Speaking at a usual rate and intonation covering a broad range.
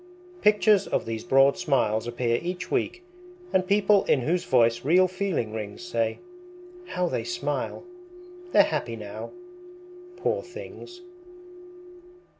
No: slow, 120 wpm; wide, 9.0 semitones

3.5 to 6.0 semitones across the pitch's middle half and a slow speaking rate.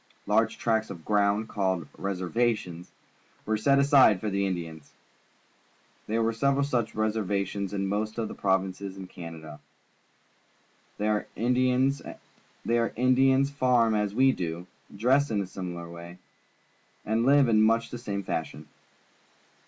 Yes: average, 4.2 semitones; slow, 130 wpm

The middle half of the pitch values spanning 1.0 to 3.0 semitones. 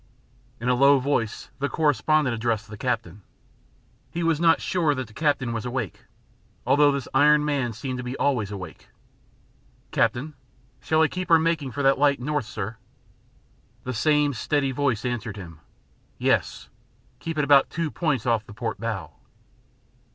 No: average, 4.4 semitones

